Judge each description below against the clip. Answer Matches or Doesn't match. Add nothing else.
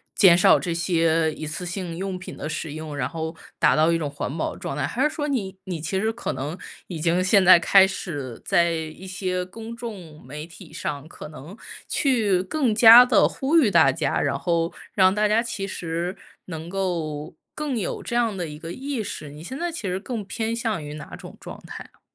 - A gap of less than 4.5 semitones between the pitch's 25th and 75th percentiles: Doesn't match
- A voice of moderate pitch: Matches